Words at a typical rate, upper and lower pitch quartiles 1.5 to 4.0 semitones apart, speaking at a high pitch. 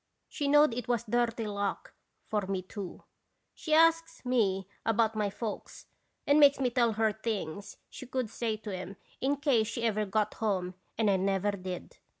Yes: average, 175 wpm; average, 3.6 semitones; high, 220 Hz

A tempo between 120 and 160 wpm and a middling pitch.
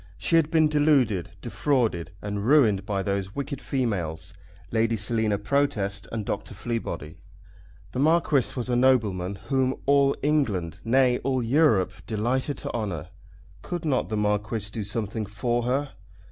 No: average, 145 wpm; low, 115 Hz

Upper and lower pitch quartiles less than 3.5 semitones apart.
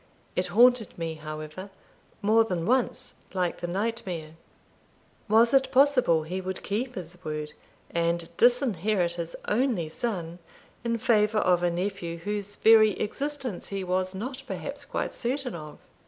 No: average, 5.3 semitones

